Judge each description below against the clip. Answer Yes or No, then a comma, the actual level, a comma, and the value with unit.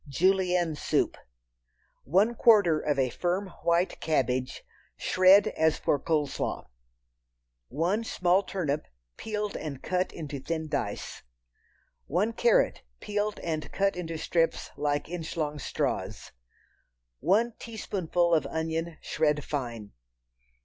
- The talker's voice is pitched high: No, medium, 165 Hz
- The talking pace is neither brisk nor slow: No, slow, 115 wpm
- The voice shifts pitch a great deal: No, average, 4.3 semitones